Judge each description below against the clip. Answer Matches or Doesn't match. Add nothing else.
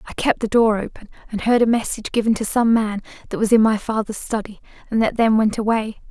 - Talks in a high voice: Matches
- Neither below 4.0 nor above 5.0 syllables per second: Doesn't match